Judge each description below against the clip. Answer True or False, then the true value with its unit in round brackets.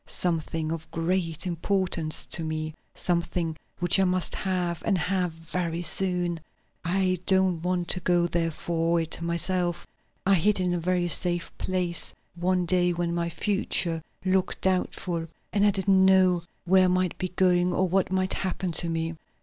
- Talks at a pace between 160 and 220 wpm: True (165 wpm)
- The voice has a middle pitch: True (175 Hz)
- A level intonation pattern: True (1.7 semitones)